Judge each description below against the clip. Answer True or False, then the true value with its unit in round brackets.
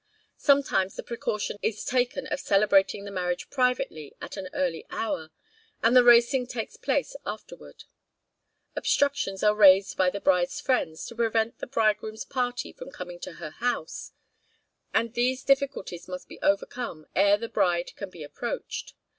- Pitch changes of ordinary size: True (5.0 semitones)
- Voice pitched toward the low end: False (215 Hz)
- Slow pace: False (155 wpm)